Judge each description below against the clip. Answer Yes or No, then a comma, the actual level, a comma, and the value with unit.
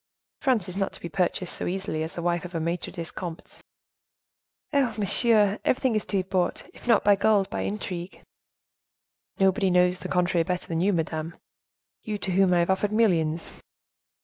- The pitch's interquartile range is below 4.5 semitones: Yes, average, 3.0 semitones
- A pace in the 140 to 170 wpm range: No, average, 190 wpm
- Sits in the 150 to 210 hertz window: Yes, medium, 185 Hz